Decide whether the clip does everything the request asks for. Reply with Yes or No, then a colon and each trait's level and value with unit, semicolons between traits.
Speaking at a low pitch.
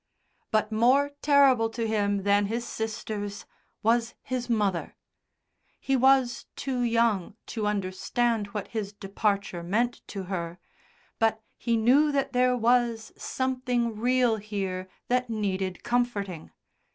No: high, 225 Hz